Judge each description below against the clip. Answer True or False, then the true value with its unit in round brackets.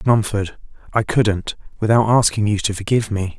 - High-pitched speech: False (105 Hz)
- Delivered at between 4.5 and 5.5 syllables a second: True (5.2 syllables/s)